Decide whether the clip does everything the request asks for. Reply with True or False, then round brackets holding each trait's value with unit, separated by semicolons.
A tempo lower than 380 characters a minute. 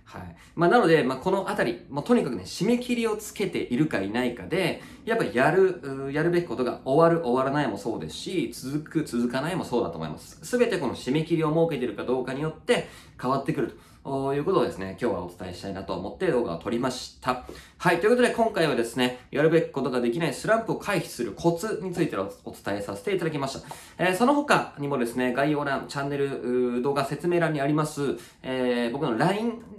False (460 characters per minute)